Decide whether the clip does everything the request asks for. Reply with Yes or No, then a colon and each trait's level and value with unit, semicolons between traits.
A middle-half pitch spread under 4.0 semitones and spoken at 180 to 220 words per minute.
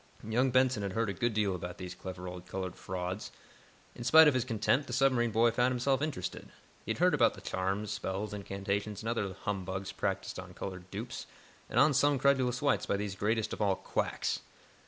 No: average, 4.6 semitones; average, 200 wpm